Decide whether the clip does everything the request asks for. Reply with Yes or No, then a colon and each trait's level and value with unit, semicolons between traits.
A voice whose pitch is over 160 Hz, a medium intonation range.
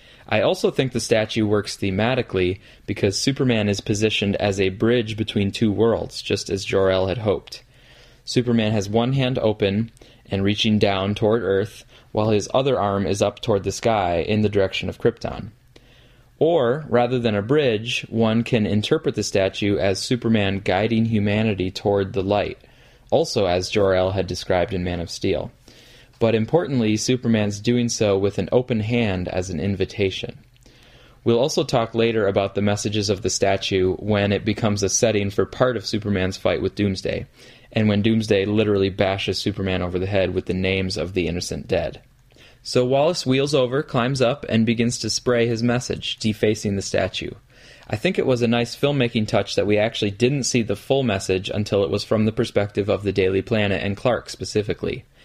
No: low, 110 Hz; average, 3.3 semitones